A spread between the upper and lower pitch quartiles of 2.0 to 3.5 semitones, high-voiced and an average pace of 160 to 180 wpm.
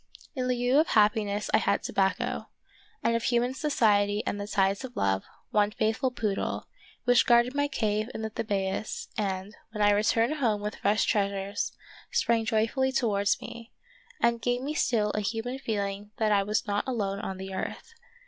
Yes: average, 2.9 semitones; high, 215 Hz; average, 175 wpm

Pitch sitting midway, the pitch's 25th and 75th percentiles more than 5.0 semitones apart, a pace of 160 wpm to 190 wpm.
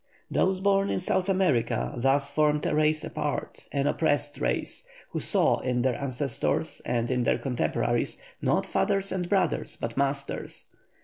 No: medium, 145 Hz; wide, 5.5 semitones; average, 150 wpm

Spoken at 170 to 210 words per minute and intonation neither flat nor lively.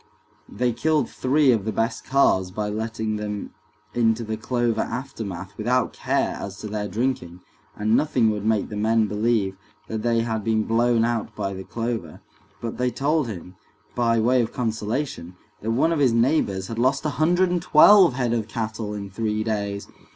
Yes: average, 180 wpm; average, 3.0 semitones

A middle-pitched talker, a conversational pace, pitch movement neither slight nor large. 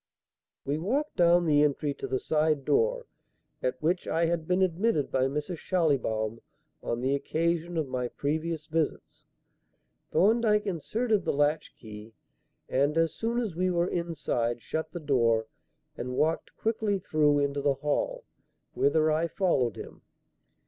Yes: medium, 160 Hz; average, 150 wpm; average, 4.3 semitones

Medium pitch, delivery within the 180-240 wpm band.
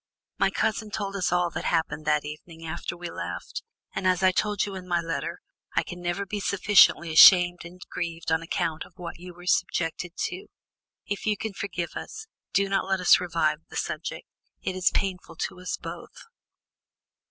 Yes: medium, 180 Hz; average, 185 wpm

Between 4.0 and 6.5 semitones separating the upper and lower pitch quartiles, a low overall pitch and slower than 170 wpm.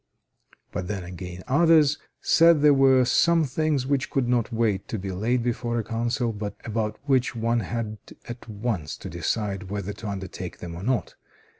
No: average, 4.4 semitones; low, 115 Hz; average, 175 wpm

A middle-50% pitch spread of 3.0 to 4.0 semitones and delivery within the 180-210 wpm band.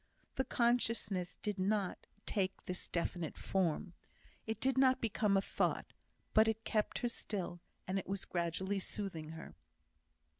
No: average, 3.6 semitones; average, 145 wpm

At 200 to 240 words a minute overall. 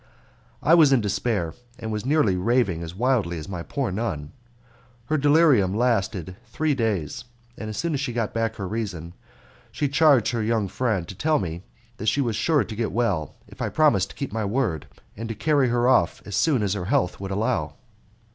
Yes: fast, 205 wpm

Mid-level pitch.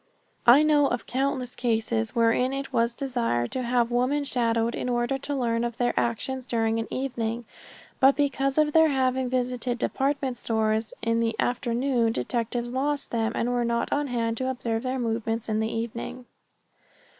No: high, 245 Hz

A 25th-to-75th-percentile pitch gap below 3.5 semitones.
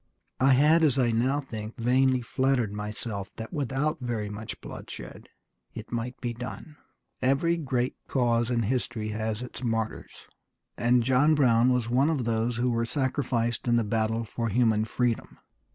Yes: narrow, 2.6 semitones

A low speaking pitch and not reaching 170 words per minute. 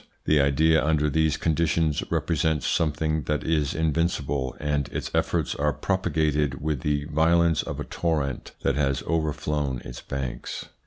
Yes: very low, 75 Hz; average, 150 wpm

